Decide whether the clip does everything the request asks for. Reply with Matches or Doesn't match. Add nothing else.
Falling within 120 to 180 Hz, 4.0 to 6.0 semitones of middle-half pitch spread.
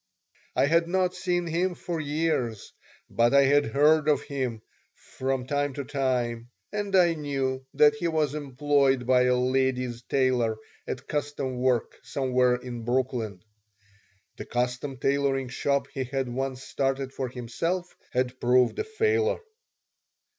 Doesn't match